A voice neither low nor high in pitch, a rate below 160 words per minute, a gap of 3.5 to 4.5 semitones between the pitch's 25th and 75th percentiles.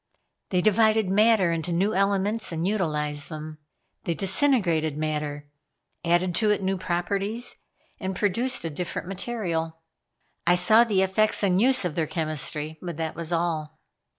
Yes: medium, 180 Hz; average, 150 wpm; average, 4.2 semitones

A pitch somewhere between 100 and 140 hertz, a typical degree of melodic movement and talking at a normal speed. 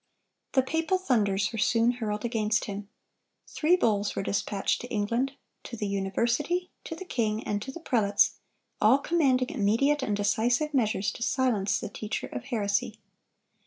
No: high, 230 Hz; average, 4.5 semitones; average, 150 wpm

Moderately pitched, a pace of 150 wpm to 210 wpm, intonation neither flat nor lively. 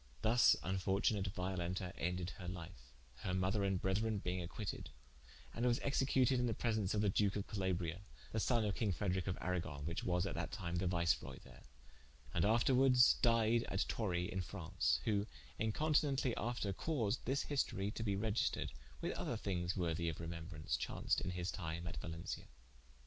No: very low, 95 Hz; average, 170 wpm; average, 4.1 semitones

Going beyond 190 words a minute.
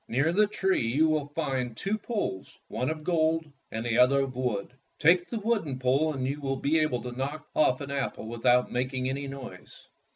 Yes: average, 200 wpm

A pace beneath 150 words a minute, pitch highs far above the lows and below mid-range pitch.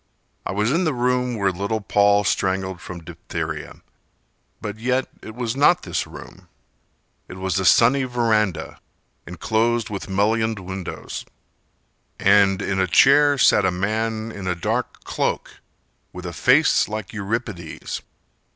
No: average, 140 wpm; average, 3.8 semitones; low, 105 Hz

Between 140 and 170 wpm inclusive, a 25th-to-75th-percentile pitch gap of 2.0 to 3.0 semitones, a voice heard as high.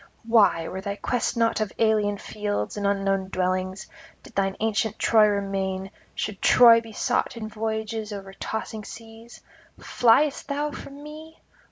Yes: average, 150 wpm; narrow, 2.6 semitones; high, 215 Hz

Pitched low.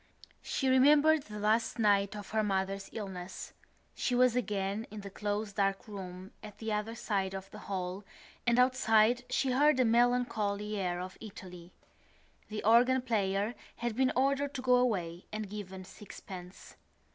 No: high, 210 Hz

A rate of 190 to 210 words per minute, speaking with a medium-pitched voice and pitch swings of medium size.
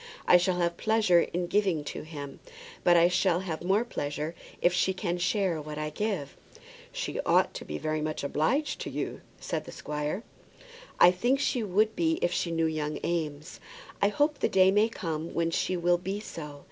Yes: average, 195 wpm; medium, 175 Hz; average, 3.9 semitones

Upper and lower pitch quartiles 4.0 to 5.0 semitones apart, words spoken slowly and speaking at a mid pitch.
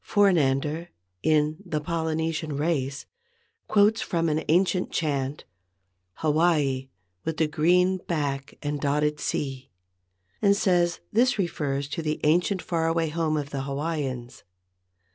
No: average, 3.1 semitones; slow, 125 wpm; medium, 155 Hz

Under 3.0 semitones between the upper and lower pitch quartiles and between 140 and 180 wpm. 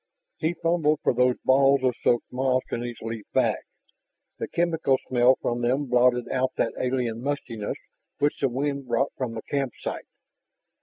Yes: narrow, 2.4 semitones; average, 160 wpm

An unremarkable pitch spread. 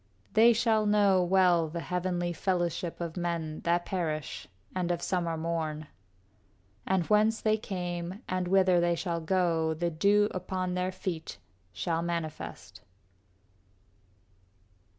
No: narrow, 2.0 semitones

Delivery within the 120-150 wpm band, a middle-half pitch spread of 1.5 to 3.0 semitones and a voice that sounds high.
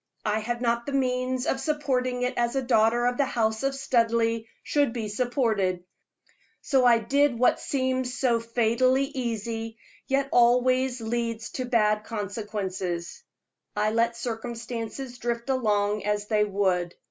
Yes: average, 145 wpm; narrow, 2.6 semitones; high, 235 Hz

